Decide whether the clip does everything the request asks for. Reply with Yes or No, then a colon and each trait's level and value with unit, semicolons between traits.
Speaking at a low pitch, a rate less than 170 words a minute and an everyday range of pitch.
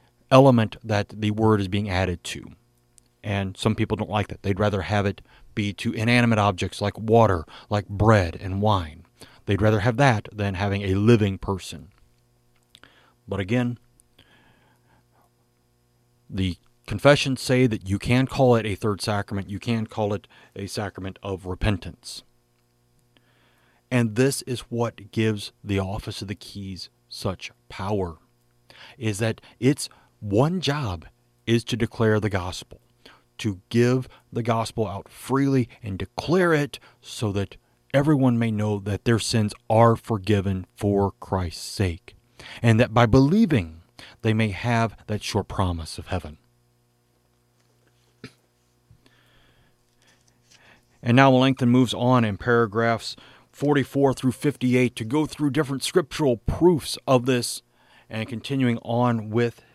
Yes: low, 110 Hz; average, 140 wpm; average, 4.2 semitones